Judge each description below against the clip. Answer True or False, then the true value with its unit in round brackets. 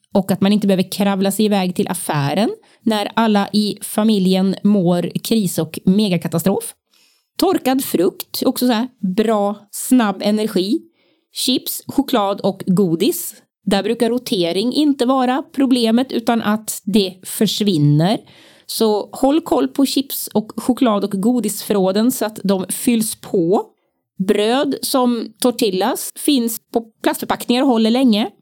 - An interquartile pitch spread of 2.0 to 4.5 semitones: True (4.2 semitones)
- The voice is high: True (220 Hz)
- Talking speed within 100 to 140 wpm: True (135 wpm)